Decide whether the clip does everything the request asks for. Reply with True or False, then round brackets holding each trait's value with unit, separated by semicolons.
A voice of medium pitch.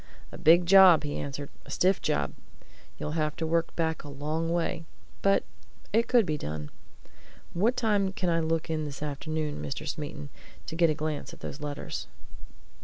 True (160 Hz)